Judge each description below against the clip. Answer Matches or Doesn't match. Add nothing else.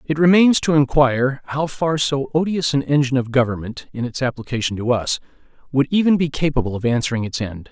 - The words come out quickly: Doesn't match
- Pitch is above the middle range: Doesn't match